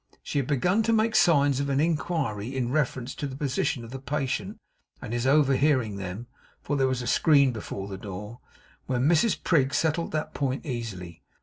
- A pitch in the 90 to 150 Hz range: Yes, low, 135 Hz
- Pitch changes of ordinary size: Yes, average, 4.0 semitones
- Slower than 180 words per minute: No, average, 185 wpm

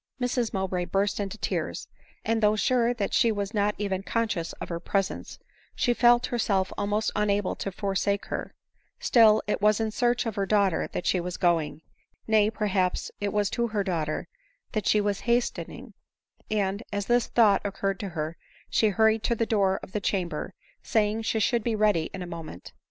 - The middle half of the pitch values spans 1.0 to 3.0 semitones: Yes, narrow, 2.4 semitones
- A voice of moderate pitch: No, high, 205 Hz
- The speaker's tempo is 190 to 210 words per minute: Yes, average, 195 wpm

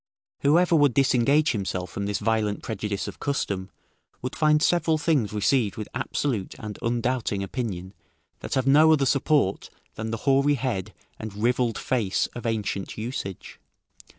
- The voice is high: No, low, 120 Hz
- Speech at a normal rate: Yes, average, 150 wpm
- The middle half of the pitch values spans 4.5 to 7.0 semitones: Yes, average, 5.2 semitones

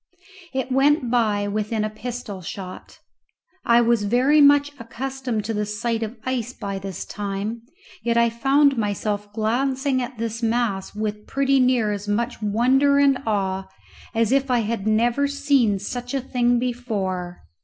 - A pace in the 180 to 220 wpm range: No, average, 155 wpm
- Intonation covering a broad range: No, average, 3.6 semitones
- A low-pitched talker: No, high, 235 Hz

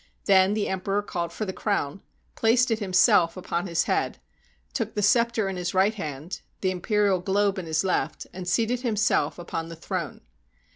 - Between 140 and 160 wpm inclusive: No, average, 180 wpm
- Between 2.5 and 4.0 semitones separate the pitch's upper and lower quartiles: Yes, average, 3.1 semitones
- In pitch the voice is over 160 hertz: Yes, high, 190 Hz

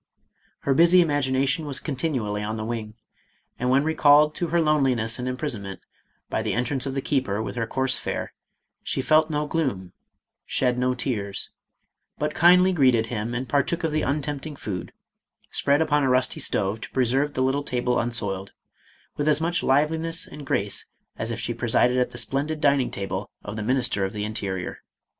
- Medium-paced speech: Yes, average, 180 wpm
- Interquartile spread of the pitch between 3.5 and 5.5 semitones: Yes, average, 4.7 semitones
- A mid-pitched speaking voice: No, low, 130 Hz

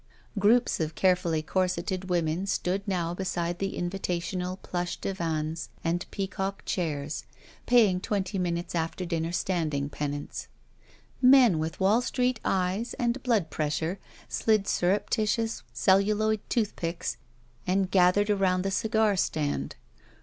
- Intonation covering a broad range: No, average, 3.2 semitones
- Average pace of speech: No, slow, 120 wpm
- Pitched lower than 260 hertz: Yes, medium, 185 Hz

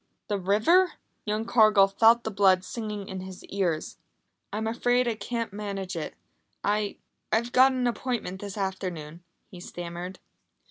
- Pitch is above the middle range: Yes, high, 205 Hz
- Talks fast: No, average, 145 wpm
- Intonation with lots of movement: No, average, 3.3 semitones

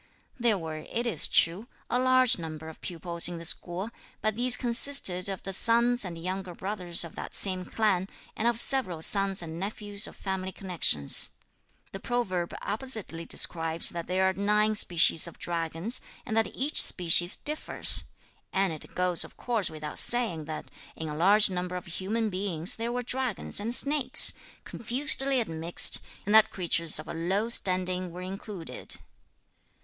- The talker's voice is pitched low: No, high, 190 Hz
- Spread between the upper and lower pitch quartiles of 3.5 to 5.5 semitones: Yes, average, 4.8 semitones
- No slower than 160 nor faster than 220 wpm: Yes, average, 165 wpm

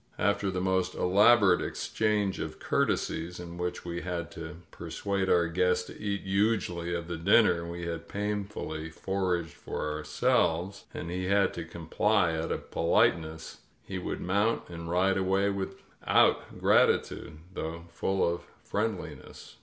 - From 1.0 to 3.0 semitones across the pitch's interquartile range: Yes, average, 2.7 semitones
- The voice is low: Yes, very low, 90 Hz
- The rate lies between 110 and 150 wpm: Yes, average, 145 wpm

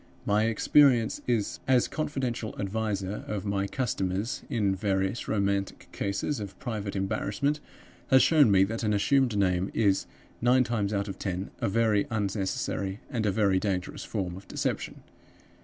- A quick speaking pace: No, average, 145 wpm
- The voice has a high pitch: No, low, 105 Hz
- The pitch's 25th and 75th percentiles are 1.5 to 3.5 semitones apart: Yes, average, 3.1 semitones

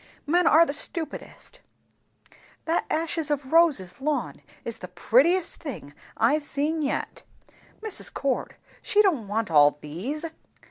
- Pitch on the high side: Yes, very high, 290 Hz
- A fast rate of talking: No, slow, 135 wpm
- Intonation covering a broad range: Yes, wide, 6.4 semitones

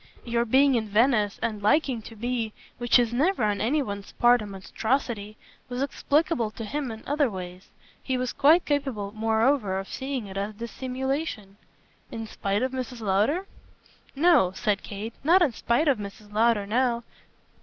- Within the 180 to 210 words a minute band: No, average, 165 wpm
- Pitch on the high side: Yes, high, 235 Hz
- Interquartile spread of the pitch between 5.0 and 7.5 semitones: No, average, 4.3 semitones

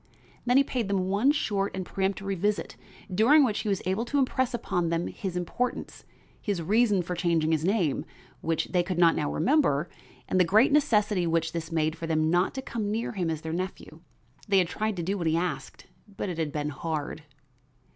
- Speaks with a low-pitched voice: No, medium, 185 Hz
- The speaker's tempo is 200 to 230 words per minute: Yes, fast, 205 wpm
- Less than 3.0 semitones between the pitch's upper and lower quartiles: No, average, 4.3 semitones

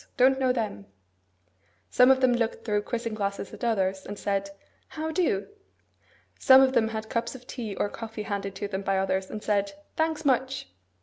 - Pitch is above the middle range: Yes, high, 220 Hz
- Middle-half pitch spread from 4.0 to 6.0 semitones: Yes, average, 4.4 semitones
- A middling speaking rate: Yes, average, 185 wpm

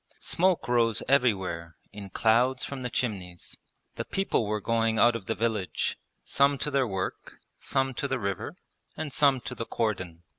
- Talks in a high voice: No, low, 115 Hz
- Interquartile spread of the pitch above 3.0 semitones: Yes, average, 4.9 semitones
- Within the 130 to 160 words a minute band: No, average, 170 wpm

